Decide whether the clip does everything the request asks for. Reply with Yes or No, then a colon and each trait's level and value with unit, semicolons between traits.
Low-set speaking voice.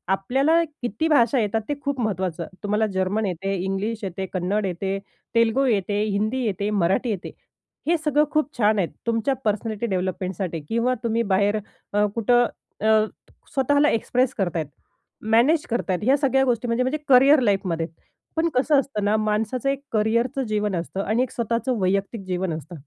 No: high, 220 Hz